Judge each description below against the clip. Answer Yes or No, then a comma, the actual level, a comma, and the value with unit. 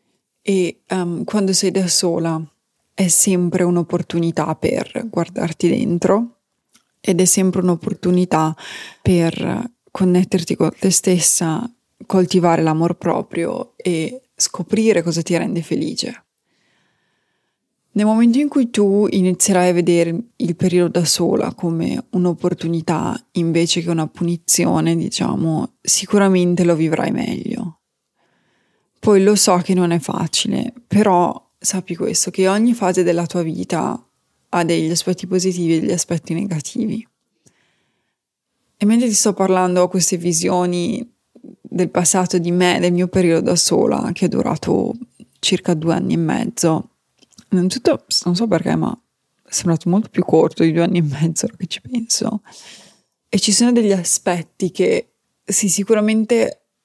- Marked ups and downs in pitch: No, average, 3.3 semitones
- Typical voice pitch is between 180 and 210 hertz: Yes, medium, 185 Hz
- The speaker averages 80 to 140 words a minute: Yes, average, 135 wpm